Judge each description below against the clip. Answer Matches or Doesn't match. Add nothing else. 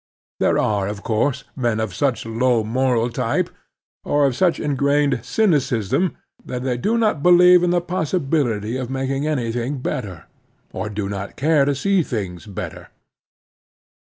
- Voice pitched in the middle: Doesn't match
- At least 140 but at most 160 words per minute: Matches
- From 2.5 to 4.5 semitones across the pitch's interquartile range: Doesn't match